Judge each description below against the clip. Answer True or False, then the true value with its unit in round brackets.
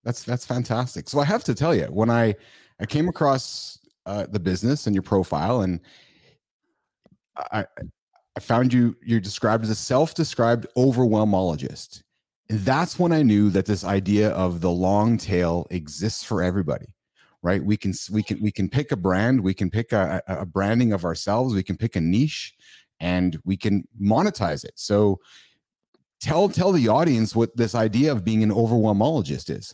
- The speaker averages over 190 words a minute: False (175 wpm)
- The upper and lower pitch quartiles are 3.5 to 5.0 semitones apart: True (4.1 semitones)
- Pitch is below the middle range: True (110 Hz)